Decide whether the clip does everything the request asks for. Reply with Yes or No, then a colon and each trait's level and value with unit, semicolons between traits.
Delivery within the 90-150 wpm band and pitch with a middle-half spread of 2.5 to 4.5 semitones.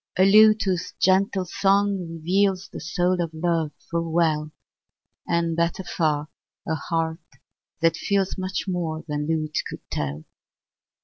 Yes: slow, 135 wpm; average, 2.8 semitones